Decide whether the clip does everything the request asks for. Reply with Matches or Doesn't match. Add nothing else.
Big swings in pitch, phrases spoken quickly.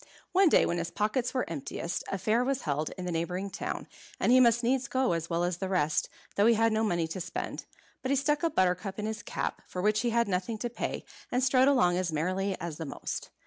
Matches